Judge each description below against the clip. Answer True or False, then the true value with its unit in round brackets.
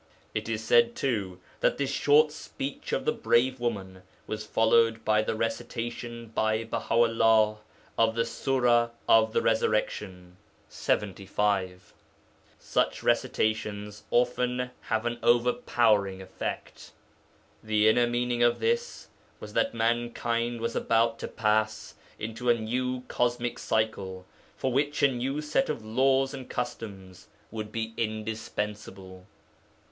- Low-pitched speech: True (115 Hz)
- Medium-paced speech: False (125 wpm)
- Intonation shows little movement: True (2.1 semitones)